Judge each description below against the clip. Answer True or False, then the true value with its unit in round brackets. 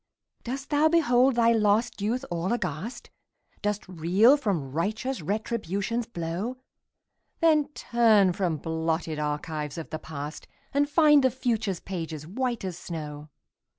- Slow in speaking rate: True (130 wpm)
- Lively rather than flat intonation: True (6.9 semitones)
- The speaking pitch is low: False (205 Hz)